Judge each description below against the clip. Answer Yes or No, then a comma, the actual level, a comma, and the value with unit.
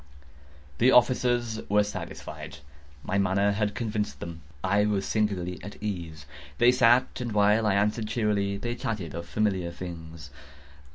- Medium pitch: No, low, 105 Hz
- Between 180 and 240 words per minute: No, average, 145 wpm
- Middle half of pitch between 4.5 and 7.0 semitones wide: No, average, 3.3 semitones